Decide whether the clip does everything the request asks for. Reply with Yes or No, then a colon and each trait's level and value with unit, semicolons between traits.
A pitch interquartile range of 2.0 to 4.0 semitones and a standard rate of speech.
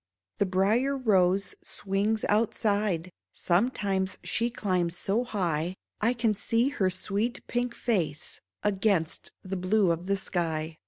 No: average, 3.5 semitones; slow, 125 wpm